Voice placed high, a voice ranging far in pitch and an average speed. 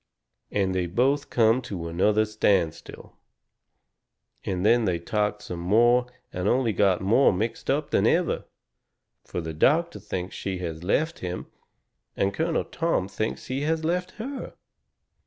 No: low, 105 Hz; wide, 6.1 semitones; average, 145 wpm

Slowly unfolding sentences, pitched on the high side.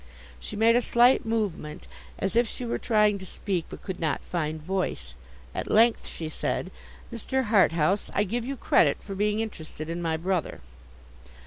No: average, 175 wpm; high, 195 Hz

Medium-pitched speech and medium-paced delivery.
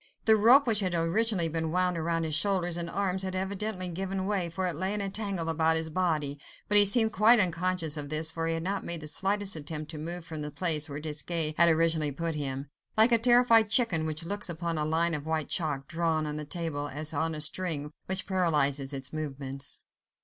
No: medium, 165 Hz; fast, 220 wpm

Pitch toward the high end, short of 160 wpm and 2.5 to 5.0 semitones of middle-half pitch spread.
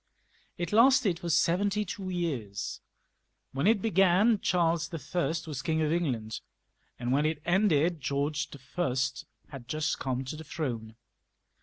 No: medium, 160 Hz; average, 140 wpm; average, 4.5 semitones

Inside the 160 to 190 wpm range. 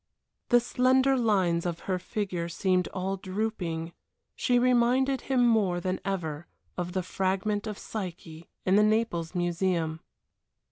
No: slow, 135 wpm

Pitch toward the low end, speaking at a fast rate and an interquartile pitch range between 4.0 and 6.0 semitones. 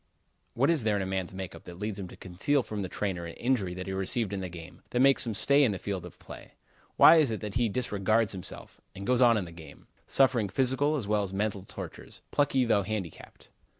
Yes: low, 105 Hz; fast, 245 wpm; average, 4.5 semitones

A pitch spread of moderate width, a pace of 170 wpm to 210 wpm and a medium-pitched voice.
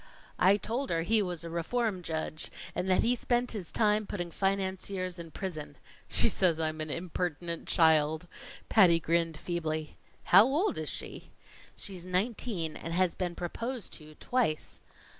No: average, 3.8 semitones; average, 155 wpm; medium, 180 Hz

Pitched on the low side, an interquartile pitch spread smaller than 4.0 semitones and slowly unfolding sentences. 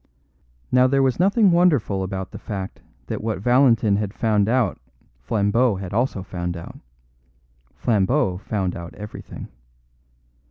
No: low, 105 Hz; average, 4.9 semitones; slow, 130 wpm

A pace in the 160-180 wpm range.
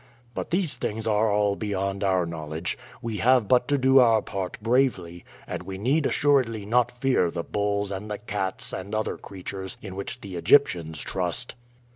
Yes: average, 175 wpm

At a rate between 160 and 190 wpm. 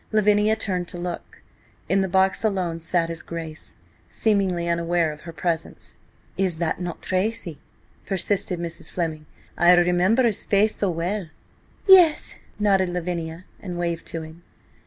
No: average, 145 wpm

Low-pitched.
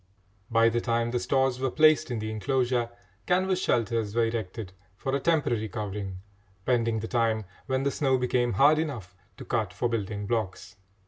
Yes: low, 120 Hz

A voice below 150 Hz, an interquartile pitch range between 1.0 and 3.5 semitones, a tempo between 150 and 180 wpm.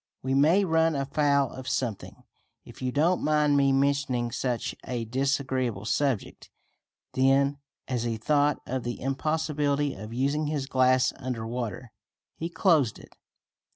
No: low, 135 Hz; average, 2.7 semitones; average, 140 wpm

